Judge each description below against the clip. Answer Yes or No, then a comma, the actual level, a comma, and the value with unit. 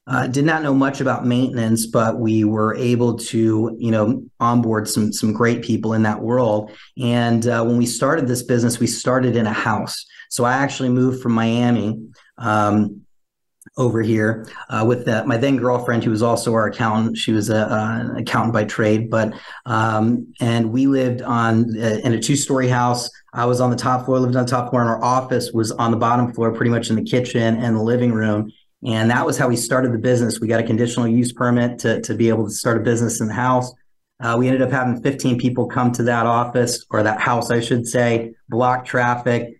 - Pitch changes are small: Yes, narrow, 1.8 semitones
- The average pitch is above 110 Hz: Yes, low, 120 Hz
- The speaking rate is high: Yes, fast, 220 wpm